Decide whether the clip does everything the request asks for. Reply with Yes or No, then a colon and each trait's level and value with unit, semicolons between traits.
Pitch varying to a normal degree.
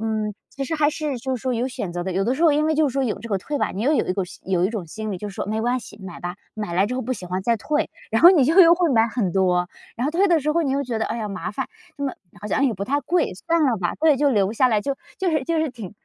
No: wide, 6.2 semitones